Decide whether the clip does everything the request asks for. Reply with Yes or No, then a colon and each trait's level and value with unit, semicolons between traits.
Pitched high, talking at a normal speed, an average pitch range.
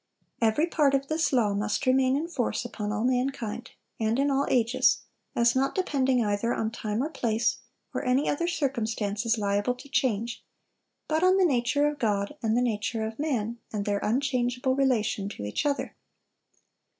Yes: high, 245 Hz; average, 175 wpm; average, 4.1 semitones